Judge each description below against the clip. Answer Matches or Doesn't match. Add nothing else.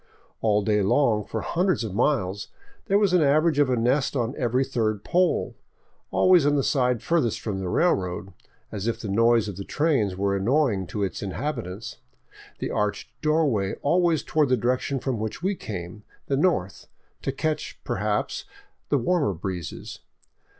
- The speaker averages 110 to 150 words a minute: Doesn't match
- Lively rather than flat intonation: Matches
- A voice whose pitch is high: Doesn't match